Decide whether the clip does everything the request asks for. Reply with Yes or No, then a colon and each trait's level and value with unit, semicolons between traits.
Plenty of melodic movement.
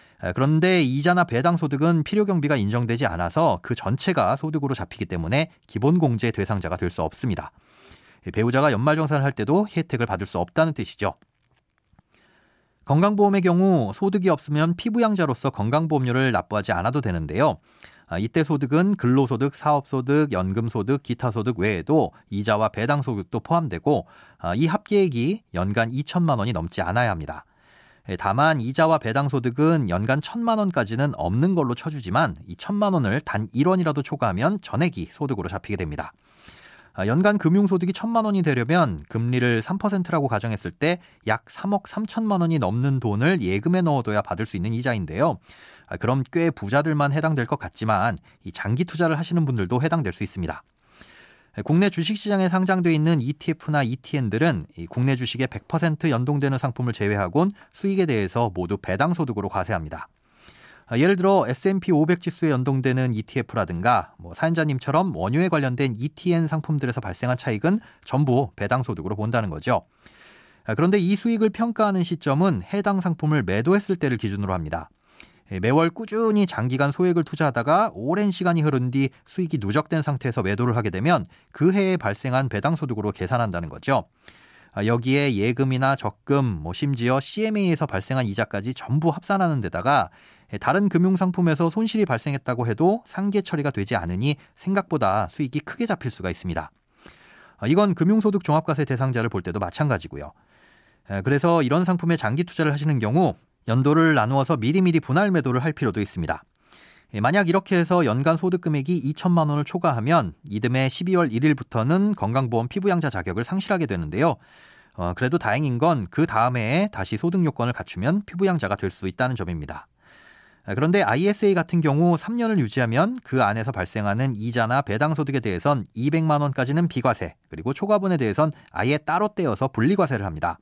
Yes: wide, 7.0 semitones